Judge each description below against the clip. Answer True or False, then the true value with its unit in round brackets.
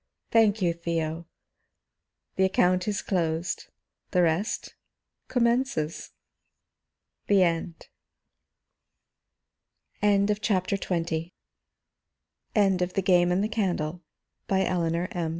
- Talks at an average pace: False (95 wpm)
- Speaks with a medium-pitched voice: True (180 Hz)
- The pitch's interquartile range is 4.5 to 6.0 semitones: False (3.1 semitones)